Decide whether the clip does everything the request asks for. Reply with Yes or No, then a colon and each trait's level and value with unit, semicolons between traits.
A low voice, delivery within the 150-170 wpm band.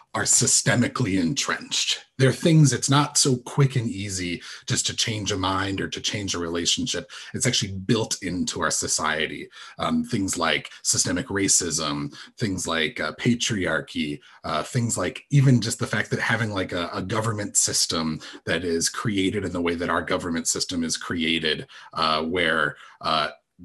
Yes: low, 100 Hz; average, 165 wpm